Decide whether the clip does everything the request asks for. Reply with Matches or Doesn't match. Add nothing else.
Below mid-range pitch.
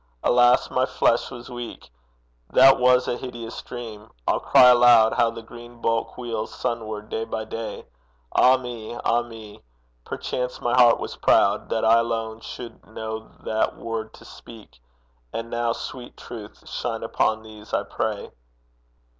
Matches